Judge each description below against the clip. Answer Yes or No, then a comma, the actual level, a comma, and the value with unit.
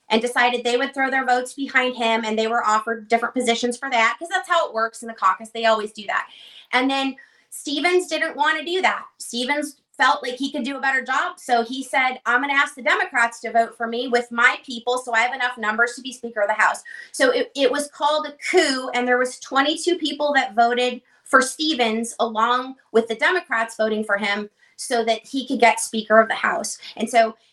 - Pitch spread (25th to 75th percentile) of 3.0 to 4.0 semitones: Yes, average, 3.3 semitones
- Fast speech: Yes, fast, 235 wpm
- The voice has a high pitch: Yes, high, 245 Hz